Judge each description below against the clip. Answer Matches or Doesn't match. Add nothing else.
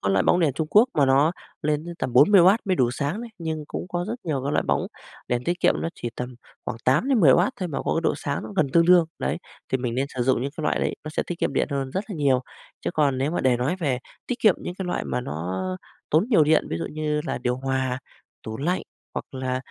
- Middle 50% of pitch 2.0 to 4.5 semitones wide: Doesn't match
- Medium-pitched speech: Matches